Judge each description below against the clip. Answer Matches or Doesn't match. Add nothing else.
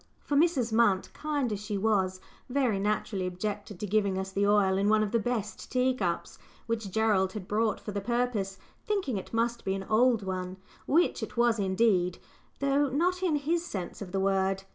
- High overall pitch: Matches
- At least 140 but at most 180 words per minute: Doesn't match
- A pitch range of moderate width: Matches